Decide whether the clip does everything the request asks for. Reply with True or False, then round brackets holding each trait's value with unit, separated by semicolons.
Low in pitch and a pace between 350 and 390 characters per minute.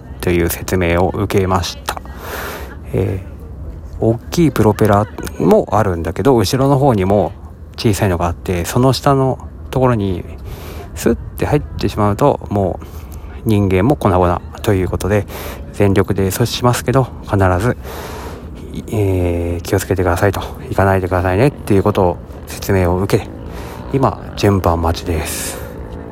False (95 Hz; 285 characters per minute)